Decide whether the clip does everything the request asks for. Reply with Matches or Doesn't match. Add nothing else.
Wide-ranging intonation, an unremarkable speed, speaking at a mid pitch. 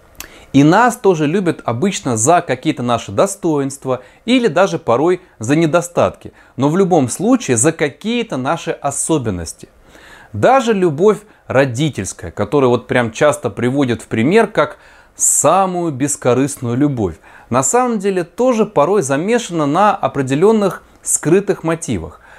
Matches